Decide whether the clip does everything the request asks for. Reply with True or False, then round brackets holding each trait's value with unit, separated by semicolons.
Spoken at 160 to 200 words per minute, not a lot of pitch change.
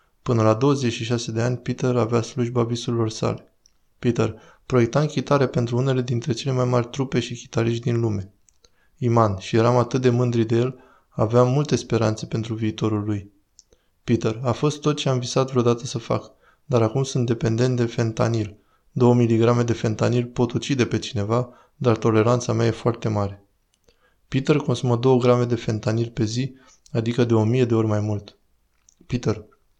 True (170 wpm; 1.9 semitones)